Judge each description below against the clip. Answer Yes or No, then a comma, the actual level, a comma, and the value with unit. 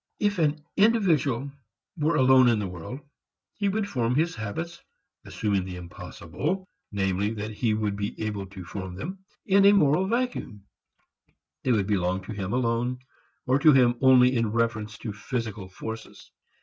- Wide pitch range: Yes, wide, 6.7 semitones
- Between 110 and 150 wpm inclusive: No, average, 160 wpm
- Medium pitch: No, low, 115 Hz